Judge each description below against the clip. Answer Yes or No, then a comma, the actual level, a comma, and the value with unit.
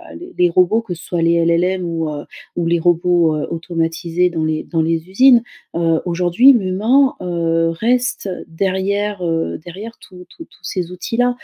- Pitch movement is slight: No, average, 3.3 semitones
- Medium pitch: Yes, medium, 175 Hz